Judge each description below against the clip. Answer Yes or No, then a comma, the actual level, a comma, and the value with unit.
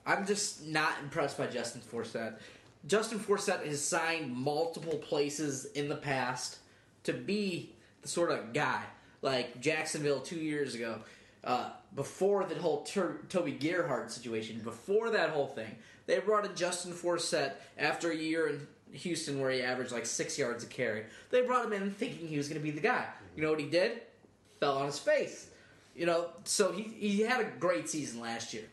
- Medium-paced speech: Yes, average, 185 wpm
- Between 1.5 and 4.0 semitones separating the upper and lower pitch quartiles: No, average, 4.9 semitones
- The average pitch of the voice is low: No, medium, 155 Hz